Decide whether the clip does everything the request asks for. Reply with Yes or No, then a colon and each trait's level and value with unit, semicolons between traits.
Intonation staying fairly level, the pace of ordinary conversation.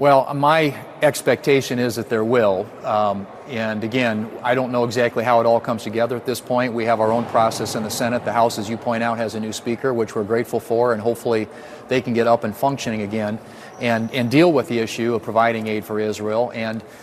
No: narrow, 1.6 semitones; fast, 230 wpm